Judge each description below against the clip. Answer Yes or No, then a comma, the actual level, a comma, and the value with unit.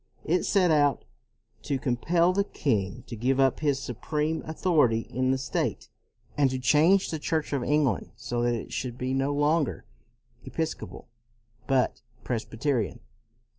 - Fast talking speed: No, average, 155 wpm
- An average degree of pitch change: Yes, average, 4.0 semitones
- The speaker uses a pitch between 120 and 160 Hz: Yes, low, 135 Hz